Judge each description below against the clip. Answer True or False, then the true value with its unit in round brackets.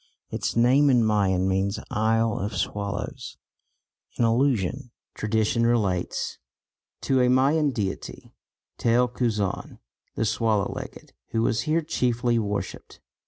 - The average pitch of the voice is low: True (115 Hz)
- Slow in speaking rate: True (120 wpm)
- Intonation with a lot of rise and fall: False (3.4 semitones)